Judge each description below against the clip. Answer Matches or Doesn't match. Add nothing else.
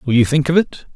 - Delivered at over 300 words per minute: Matches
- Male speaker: Matches